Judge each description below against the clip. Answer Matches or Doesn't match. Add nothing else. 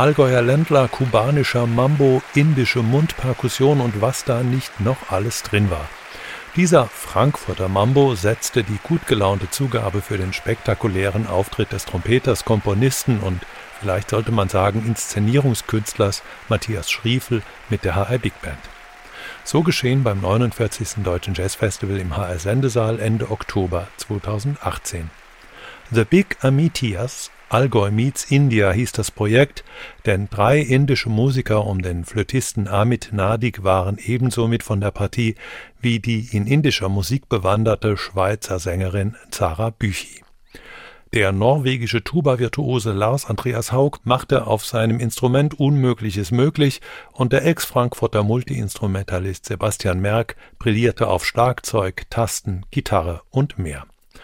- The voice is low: Matches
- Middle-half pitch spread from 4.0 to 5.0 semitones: Matches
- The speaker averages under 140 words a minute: Matches